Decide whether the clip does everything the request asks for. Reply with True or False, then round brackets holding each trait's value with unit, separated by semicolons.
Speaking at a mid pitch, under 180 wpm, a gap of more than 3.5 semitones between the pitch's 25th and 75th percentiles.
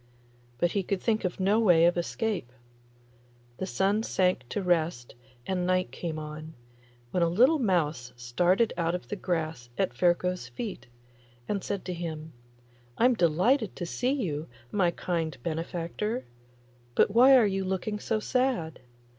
True (180 Hz; 155 wpm; 4.2 semitones)